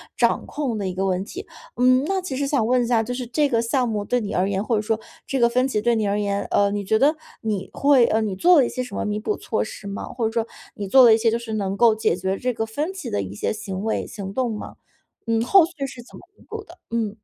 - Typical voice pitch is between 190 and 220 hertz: No, high, 230 Hz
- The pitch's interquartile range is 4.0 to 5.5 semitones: No, average, 3.6 semitones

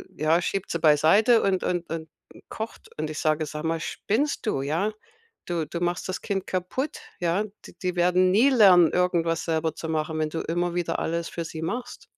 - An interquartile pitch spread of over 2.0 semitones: Yes, narrow, 2.6 semitones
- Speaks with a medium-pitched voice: Yes, medium, 170 Hz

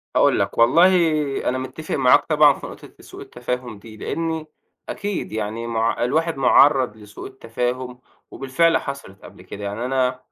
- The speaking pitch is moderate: No, low, 130 Hz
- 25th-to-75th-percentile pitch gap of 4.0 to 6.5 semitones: Yes, average, 4.3 semitones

